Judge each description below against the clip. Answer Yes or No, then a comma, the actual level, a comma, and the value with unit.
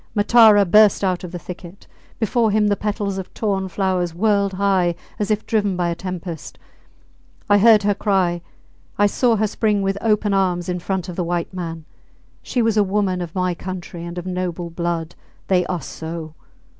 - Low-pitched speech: No, high, 190 Hz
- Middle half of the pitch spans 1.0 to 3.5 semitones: Yes, average, 2.7 semitones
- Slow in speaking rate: No, average, 185 wpm